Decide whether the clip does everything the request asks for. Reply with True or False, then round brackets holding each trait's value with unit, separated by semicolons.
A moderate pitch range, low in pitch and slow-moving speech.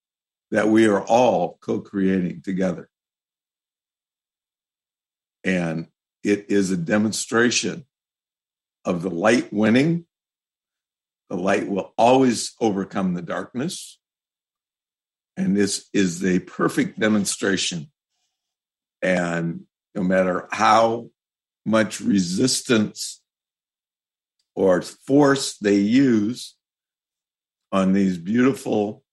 True (3.3 semitones; 100 Hz; 85 wpm)